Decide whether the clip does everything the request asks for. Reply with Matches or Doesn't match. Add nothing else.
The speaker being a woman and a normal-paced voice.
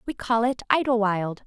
Matches